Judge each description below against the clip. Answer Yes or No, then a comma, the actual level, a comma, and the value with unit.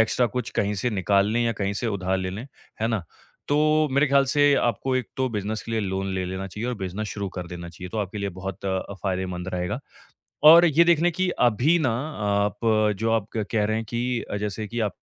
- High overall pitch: No, low, 105 Hz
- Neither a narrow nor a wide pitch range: Yes, average, 4.3 semitones